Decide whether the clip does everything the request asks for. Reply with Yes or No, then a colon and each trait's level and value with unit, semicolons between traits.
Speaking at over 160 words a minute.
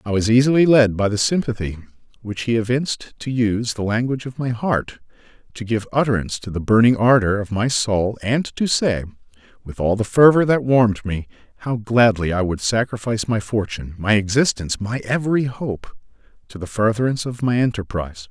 Yes: average, 180 wpm